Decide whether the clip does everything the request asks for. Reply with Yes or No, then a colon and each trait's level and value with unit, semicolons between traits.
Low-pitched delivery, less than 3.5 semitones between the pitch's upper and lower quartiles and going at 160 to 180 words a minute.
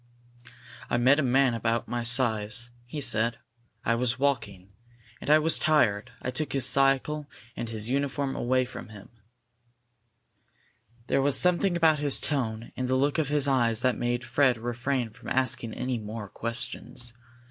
Yes: low, 125 Hz; average, 3.1 semitones; average, 165 wpm